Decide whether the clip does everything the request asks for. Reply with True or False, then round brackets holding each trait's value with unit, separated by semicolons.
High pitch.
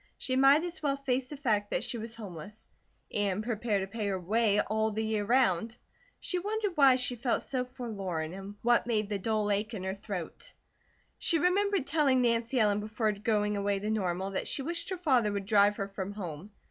True (220 Hz)